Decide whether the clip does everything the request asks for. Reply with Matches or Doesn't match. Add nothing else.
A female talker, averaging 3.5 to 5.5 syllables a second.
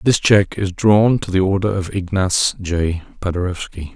Doesn't match